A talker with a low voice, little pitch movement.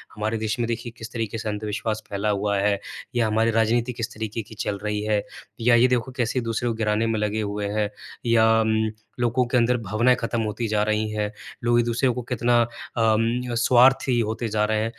Yes: low, 110 Hz; narrow, 1.8 semitones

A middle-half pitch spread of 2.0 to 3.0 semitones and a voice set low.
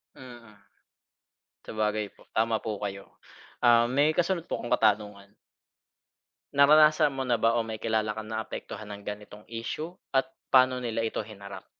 No: average, 3.4 semitones; low, 115 Hz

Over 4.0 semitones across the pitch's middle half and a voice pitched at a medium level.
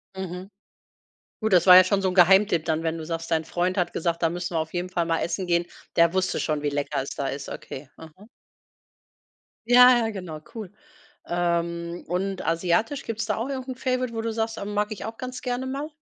Yes: average, 4.9 semitones; medium, 180 Hz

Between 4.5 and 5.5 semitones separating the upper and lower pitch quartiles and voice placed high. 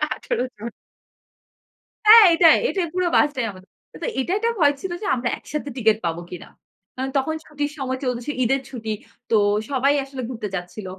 Yes: average, 4.8 semitones; very high, 265 Hz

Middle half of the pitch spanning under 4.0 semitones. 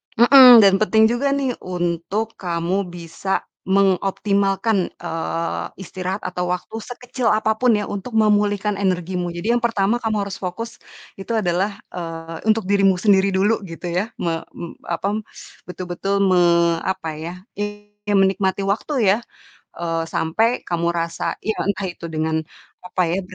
Yes: average, 3.2 semitones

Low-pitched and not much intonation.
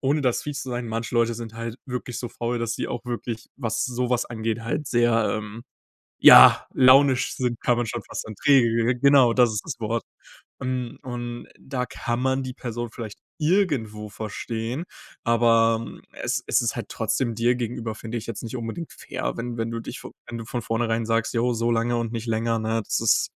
Yes: low, 120 Hz; narrow, 1.5 semitones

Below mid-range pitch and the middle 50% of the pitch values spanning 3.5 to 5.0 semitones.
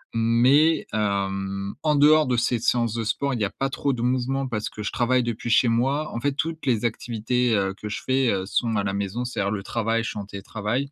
Yes: low, 115 Hz; average, 3.8 semitones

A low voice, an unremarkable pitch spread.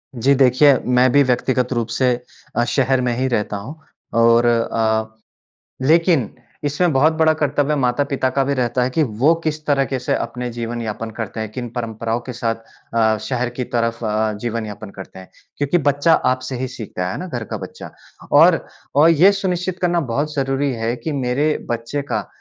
Yes: low, 125 Hz; average, 3.7 semitones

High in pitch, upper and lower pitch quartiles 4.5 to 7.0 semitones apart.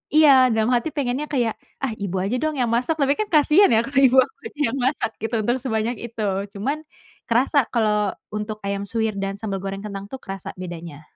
Yes: high, 230 Hz; average, 5.0 semitones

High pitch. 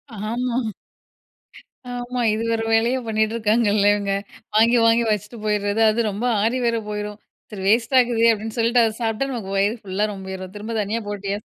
Yes: high, 220 Hz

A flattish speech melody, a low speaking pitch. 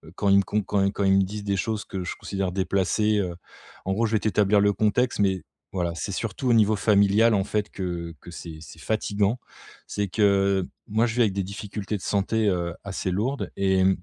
Yes: narrow, 1.9 semitones; low, 100 Hz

